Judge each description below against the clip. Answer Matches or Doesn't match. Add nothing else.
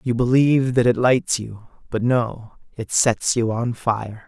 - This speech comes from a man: Matches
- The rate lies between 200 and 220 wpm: Doesn't match